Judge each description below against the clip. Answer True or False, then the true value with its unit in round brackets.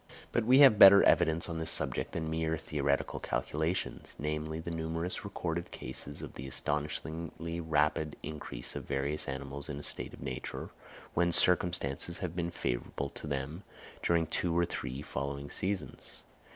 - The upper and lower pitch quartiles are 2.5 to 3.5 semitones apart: True (3.1 semitones)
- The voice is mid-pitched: False (80 Hz)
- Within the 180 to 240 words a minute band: False (155 wpm)